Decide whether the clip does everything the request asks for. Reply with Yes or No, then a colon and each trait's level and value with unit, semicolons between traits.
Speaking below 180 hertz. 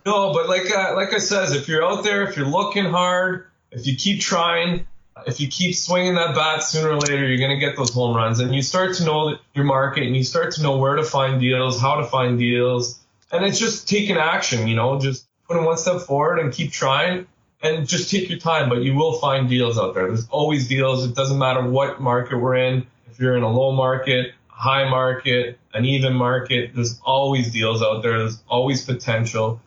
Yes: low, 135 Hz